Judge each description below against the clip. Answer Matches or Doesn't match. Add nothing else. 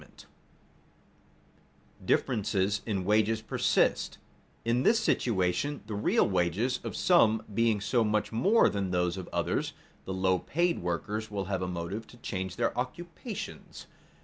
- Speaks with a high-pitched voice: Doesn't match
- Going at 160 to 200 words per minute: Doesn't match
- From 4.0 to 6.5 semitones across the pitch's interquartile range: Matches